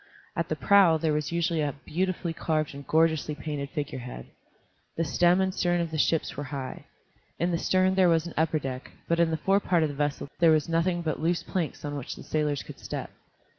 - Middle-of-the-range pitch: Yes, medium, 160 Hz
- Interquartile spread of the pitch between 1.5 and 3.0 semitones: Yes, average, 2.7 semitones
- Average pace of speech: No, fast, 215 wpm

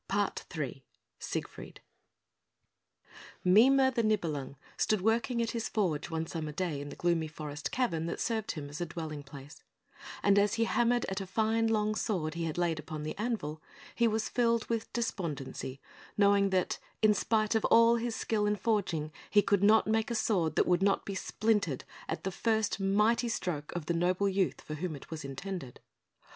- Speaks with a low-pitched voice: No, high, 195 Hz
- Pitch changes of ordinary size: No, wide, 5.7 semitones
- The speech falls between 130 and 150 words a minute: No, average, 185 wpm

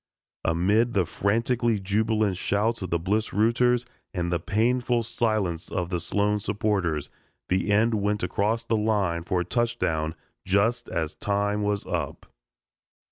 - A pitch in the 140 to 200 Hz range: No, low, 105 Hz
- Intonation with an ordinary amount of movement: Yes, average, 3.8 semitones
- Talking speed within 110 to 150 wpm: Yes, average, 140 wpm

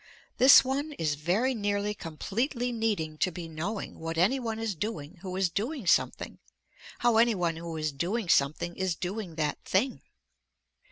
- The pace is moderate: Yes, average, 165 wpm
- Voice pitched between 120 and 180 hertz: No, high, 190 Hz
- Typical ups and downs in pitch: No, wide, 5.7 semitones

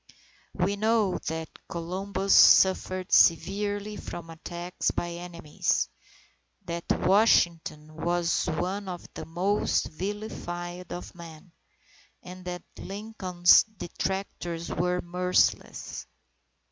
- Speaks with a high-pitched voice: No, medium, 180 Hz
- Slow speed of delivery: Yes, slow, 95 wpm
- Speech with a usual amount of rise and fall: No, narrow, 2.3 semitones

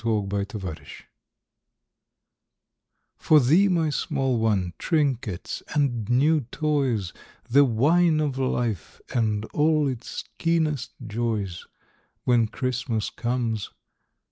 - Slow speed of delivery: Yes, slow, 100 wpm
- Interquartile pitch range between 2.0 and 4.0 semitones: No, average, 5.2 semitones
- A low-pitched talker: Yes, low, 125 Hz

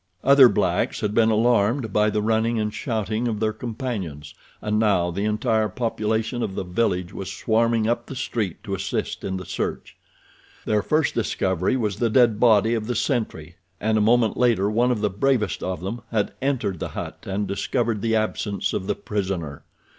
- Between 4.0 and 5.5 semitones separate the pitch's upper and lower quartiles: No, average, 2.9 semitones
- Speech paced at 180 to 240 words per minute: Yes, average, 185 wpm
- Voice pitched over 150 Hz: No, low, 110 Hz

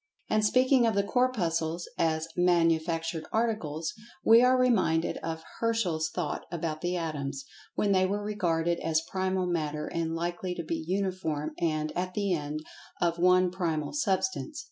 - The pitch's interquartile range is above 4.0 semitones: No, average, 3.5 semitones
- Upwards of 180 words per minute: No, average, 150 wpm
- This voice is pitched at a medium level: Yes, medium, 175 Hz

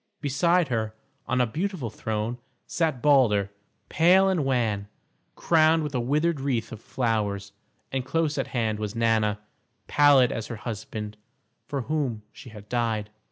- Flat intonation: No, average, 5.2 semitones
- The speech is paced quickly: No, average, 150 wpm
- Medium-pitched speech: No, low, 125 Hz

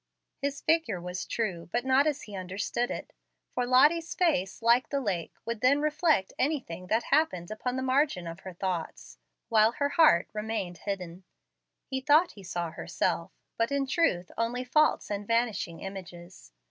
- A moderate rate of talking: Yes, average, 165 wpm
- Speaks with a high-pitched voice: Yes, high, 230 Hz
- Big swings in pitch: Yes, wide, 7.2 semitones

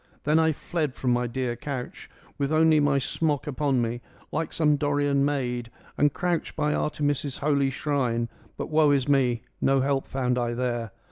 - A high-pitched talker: No, medium, 140 Hz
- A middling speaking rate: Yes, average, 180 wpm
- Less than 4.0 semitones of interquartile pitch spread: Yes, average, 3.1 semitones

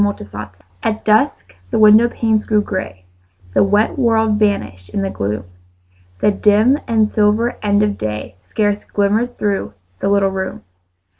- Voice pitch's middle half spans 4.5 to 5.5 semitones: No, narrow, 2.4 semitones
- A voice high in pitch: Yes, high, 205 Hz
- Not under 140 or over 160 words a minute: Yes, average, 150 wpm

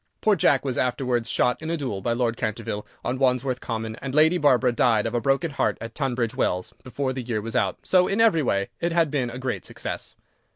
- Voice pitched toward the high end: No, low, 125 Hz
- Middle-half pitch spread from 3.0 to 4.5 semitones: Yes, average, 3.5 semitones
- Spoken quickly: Yes, fast, 225 wpm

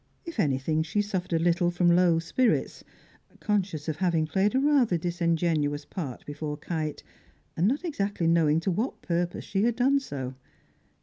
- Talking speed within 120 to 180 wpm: Yes, average, 165 wpm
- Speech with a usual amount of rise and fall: Yes, average, 4.6 semitones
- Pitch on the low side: No, medium, 175 Hz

